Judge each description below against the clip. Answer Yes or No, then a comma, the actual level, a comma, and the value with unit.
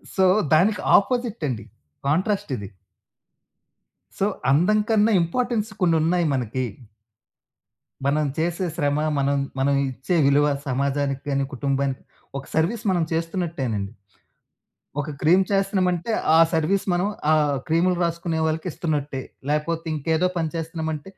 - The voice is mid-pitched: Yes, medium, 160 Hz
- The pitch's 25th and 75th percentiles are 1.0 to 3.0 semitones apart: No, average, 4.4 semitones